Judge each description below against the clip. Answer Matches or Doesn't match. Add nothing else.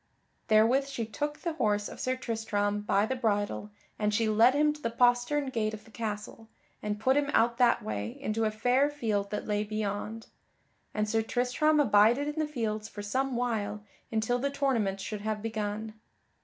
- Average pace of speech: Matches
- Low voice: Doesn't match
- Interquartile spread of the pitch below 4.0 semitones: Matches